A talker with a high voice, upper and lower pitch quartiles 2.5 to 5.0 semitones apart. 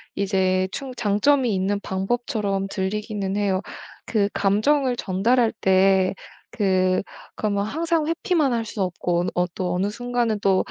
Yes: high, 205 Hz; average, 4.2 semitones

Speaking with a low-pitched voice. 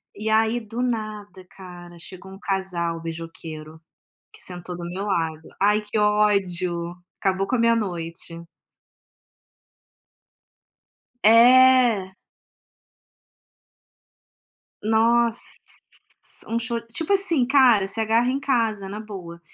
No: high, 205 Hz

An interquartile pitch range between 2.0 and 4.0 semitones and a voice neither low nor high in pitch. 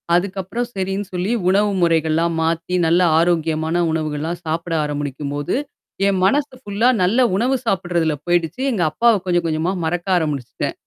Yes: average, 3.5 semitones; medium, 175 Hz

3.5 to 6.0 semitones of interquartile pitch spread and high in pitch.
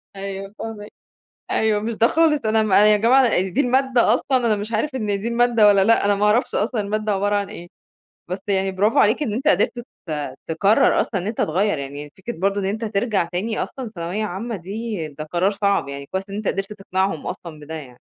No: average, 3.0 semitones; high, 205 Hz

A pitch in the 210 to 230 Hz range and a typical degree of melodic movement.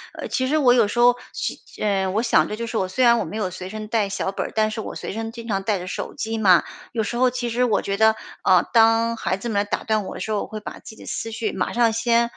No: high, 220 Hz; narrow, 2.3 semitones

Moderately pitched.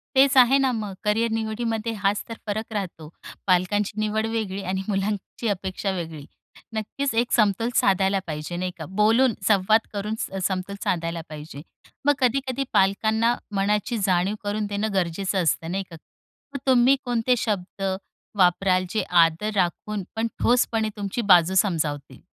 No: high, 205 Hz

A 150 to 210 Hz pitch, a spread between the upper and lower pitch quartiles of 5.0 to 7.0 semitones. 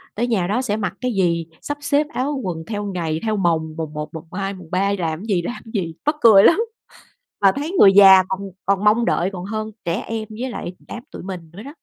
No: high, 195 Hz; average, 4.4 semitones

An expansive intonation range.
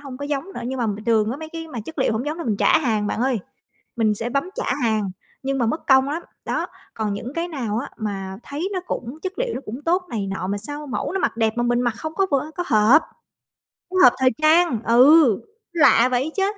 Yes: wide, 5.8 semitones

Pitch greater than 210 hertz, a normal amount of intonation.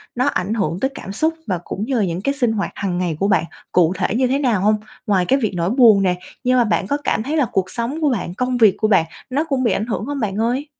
Yes: high, 220 Hz; average, 5.0 semitones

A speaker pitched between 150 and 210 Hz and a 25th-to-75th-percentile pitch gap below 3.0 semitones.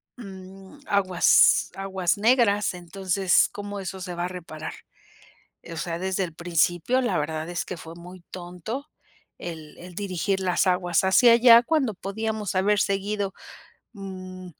Yes: high, 190 Hz; narrow, 2.5 semitones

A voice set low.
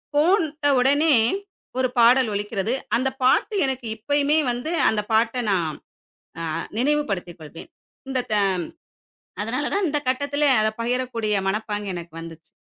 No: high, 245 Hz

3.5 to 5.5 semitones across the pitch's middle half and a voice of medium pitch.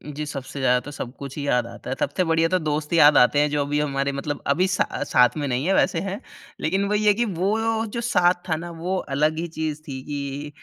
Yes: average, 4.0 semitones; medium, 150 Hz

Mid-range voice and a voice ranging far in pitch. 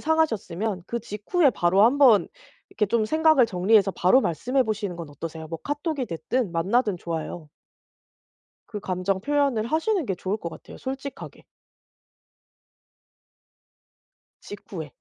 No: high, 210 Hz; wide, 6.9 semitones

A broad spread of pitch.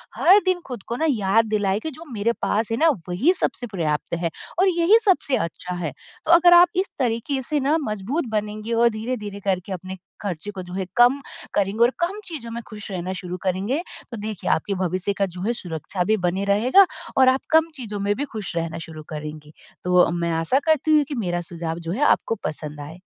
Yes: wide, 6.6 semitones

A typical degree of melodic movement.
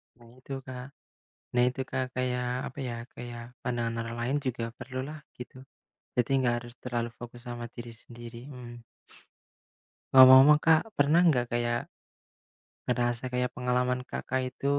No: narrow, 1.4 semitones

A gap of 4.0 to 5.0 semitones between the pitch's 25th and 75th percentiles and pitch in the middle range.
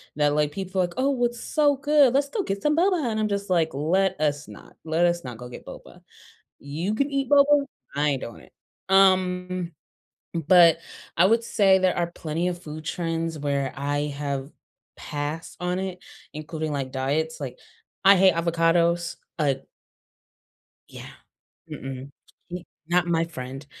Yes: average, 4.6 semitones; medium, 170 Hz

